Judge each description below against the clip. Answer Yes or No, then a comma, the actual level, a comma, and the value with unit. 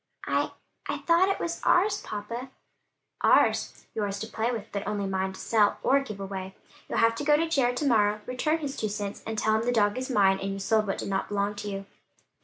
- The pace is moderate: No, fast, 230 wpm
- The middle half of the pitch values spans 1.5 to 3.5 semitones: No, average, 4.3 semitones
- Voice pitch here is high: Yes, high, 215 Hz